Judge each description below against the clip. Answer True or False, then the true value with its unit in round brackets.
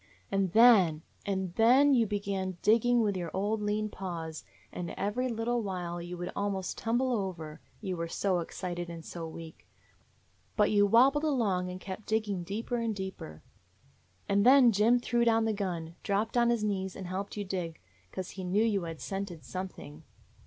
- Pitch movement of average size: True (3.9 semitones)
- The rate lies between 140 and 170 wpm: False (180 wpm)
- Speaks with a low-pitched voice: False (200 Hz)